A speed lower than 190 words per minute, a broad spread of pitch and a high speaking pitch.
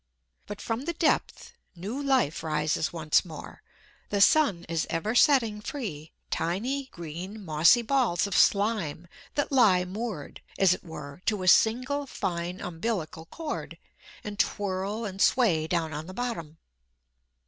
Yes: average, 140 wpm; wide, 6.0 semitones; high, 195 Hz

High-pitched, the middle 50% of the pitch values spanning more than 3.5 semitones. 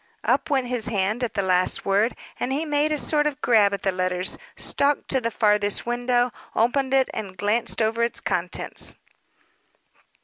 Yes: high, 235 Hz; average, 4.6 semitones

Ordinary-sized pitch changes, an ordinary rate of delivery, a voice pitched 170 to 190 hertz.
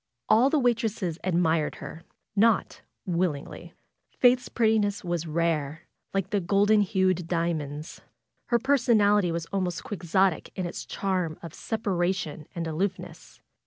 No: average, 3.8 semitones; slow, 125 wpm; medium, 185 Hz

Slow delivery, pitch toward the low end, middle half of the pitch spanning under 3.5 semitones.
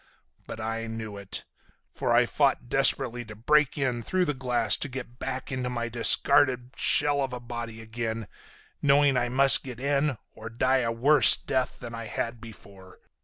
No: average, 175 wpm; low, 120 Hz; average, 2.7 semitones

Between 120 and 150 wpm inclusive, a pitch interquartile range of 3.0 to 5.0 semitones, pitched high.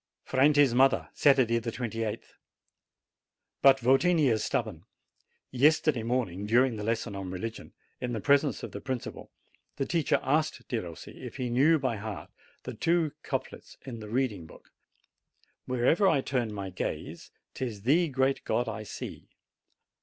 No: average, 145 wpm; average, 3.6 semitones; low, 125 Hz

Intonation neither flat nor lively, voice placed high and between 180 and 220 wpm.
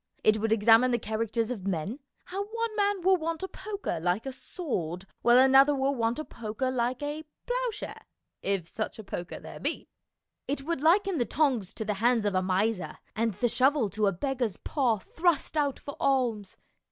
No: wide, 5.9 semitones; high, 245 Hz; average, 190 wpm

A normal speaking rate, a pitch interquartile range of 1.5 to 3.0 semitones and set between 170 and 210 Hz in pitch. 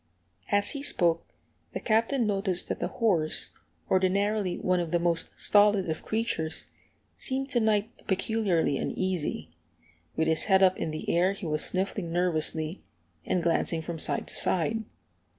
No: average, 150 wpm; average, 4.1 semitones; medium, 185 Hz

